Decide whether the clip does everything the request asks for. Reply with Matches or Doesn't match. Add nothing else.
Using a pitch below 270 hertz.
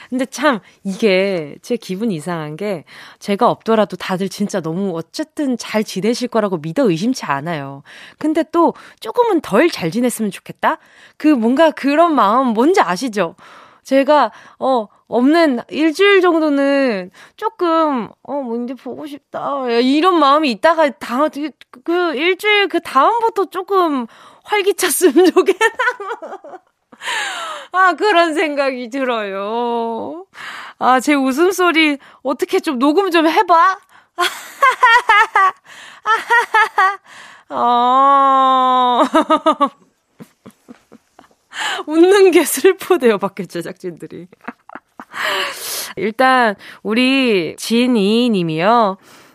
Doesn't match